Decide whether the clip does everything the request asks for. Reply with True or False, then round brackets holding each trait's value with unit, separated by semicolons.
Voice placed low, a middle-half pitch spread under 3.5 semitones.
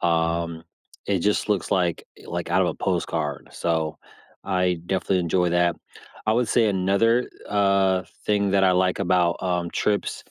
True (90 Hz; 2.5 semitones)